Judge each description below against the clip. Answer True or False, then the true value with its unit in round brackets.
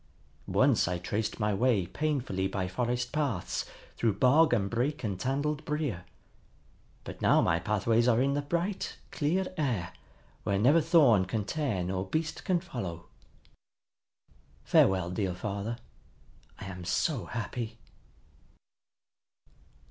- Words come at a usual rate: False (125 wpm)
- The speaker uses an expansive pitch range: True (7.2 semitones)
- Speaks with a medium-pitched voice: False (115 Hz)